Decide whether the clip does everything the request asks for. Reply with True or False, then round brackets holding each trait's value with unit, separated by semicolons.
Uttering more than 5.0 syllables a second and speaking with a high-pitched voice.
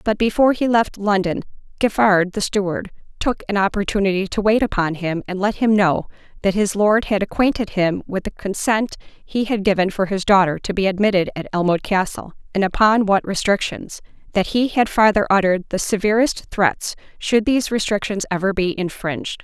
True (5.4 syllables/s; 200 Hz)